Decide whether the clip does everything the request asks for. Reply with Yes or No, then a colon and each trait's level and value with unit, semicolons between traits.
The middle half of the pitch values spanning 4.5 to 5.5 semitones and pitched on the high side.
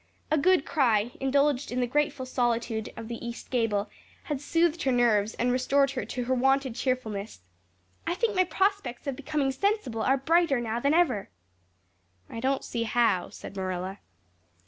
No: average, 3.8 semitones; very high, 255 Hz